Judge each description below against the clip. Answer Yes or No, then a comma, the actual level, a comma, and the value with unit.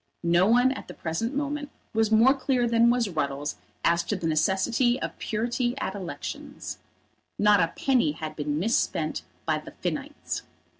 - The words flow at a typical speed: Yes, average, 160 wpm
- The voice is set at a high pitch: Yes, high, 220 Hz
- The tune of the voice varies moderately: No, wide, 6.5 semitones